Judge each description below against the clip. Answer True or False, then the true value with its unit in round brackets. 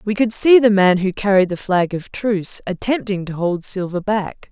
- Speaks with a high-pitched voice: True (200 Hz)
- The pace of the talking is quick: True (215 wpm)